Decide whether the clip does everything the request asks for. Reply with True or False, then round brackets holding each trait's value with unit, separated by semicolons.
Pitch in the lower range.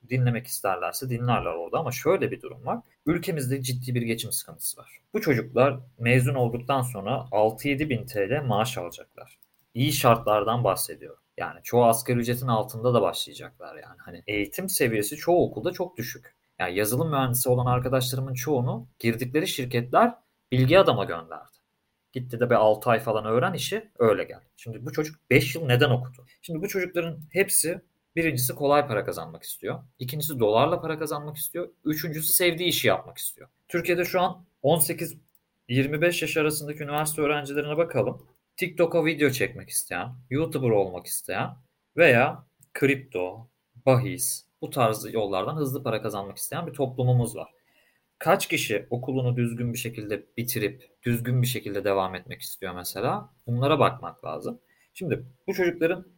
True (130 Hz)